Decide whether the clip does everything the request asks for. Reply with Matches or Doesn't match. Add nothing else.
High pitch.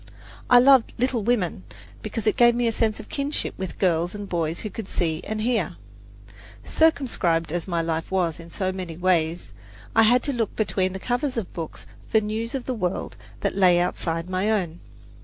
Matches